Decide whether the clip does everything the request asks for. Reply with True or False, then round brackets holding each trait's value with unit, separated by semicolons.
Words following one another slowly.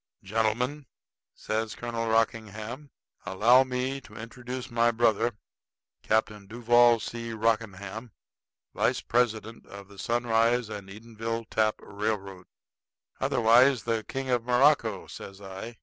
True (115 wpm)